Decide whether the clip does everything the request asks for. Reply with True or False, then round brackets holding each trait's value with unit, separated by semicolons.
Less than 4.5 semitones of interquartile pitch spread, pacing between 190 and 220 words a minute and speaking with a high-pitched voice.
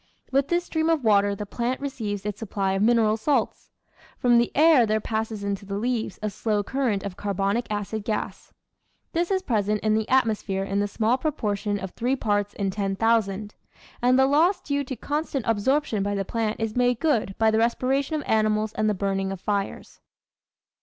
True (3.9 semitones; 200 wpm; 220 Hz)